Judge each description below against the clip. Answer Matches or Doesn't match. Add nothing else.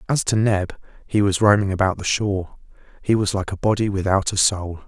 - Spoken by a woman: Doesn't match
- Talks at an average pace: Doesn't match